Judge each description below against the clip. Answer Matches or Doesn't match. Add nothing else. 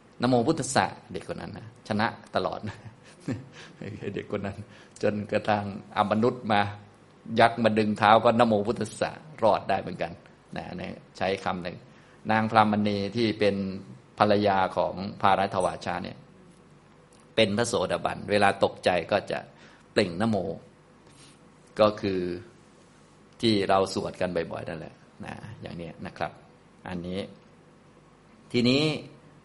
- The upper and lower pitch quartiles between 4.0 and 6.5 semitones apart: Doesn't match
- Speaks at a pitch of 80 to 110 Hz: Matches